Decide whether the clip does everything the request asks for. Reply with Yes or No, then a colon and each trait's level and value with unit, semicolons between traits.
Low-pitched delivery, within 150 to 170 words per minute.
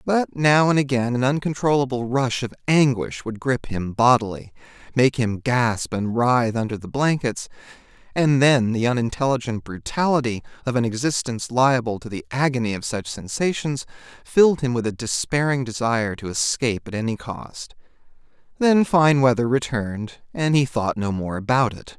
Yes: low, 125 Hz; average, 160 wpm